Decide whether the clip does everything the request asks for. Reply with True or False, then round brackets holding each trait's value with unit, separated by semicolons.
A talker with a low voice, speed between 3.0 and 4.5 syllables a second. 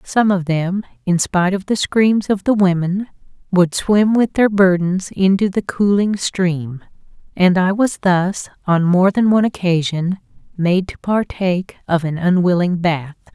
False (185 Hz; 4.3 syllables/s)